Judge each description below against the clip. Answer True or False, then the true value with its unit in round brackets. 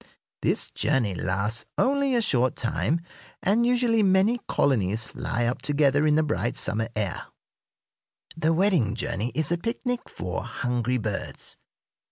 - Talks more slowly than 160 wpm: True (140 wpm)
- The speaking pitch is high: False (140 Hz)